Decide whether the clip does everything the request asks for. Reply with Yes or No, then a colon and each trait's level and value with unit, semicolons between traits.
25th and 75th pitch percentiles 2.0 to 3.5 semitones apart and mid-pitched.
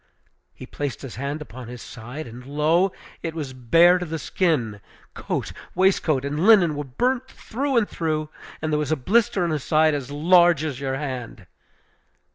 No: average, 4.6 semitones; medium, 150 Hz